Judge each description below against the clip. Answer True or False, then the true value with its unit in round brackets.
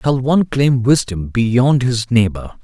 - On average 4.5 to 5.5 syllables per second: False (3.9 syllables/s)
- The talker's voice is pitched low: True (120 Hz)